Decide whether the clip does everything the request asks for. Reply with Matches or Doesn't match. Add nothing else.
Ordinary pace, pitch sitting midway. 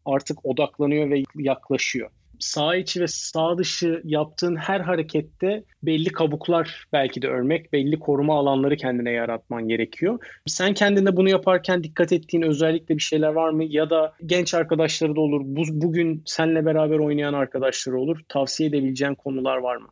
Doesn't match